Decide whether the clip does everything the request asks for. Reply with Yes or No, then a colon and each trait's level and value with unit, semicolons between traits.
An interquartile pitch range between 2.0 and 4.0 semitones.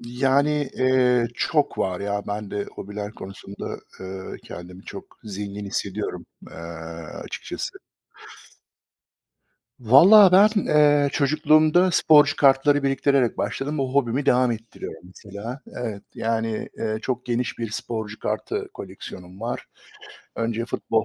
No: average, 5.3 semitones